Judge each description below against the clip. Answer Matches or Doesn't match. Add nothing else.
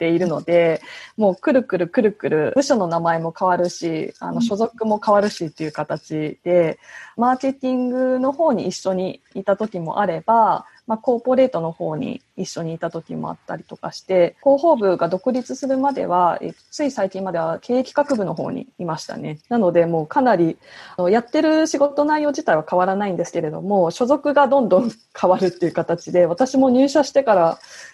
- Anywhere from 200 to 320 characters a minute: Doesn't match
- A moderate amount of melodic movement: Doesn't match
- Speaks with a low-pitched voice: Doesn't match